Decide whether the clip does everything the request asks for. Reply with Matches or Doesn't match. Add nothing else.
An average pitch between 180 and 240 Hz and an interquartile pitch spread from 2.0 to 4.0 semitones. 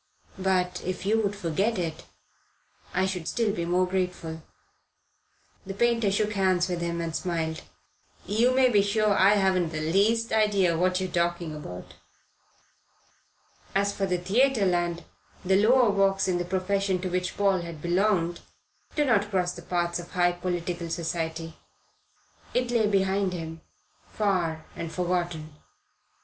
Matches